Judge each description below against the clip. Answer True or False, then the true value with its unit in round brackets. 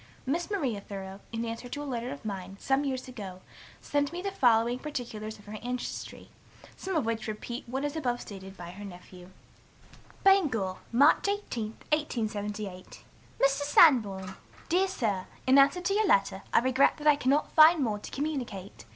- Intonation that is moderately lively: False (6.0 semitones)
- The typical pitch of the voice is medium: False (245 Hz)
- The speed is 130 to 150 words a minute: False (170 wpm)